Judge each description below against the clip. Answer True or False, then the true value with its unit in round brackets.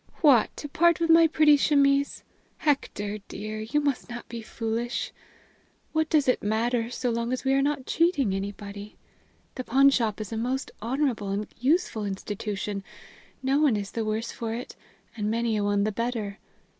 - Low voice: False (235 Hz)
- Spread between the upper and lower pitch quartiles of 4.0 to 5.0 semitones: True (4.6 semitones)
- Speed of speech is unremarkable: True (170 wpm)